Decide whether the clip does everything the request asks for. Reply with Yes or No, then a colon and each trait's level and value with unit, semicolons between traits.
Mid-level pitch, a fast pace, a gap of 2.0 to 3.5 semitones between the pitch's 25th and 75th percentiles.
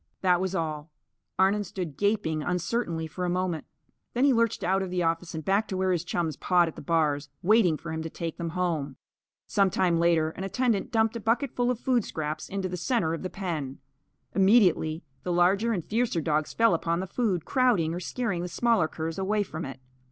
No: medium, 180 Hz; fast, 210 wpm; average, 4.0 semitones